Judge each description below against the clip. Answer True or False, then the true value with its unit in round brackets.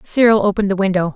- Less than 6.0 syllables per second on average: False (7.6 syllables/s)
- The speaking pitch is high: True (200 Hz)